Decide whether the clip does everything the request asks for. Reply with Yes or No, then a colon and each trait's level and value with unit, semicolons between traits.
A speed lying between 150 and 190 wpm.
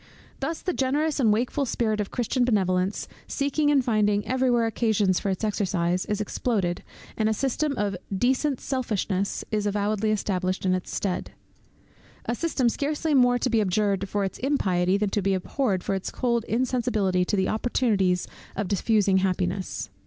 Yes: average, 165 wpm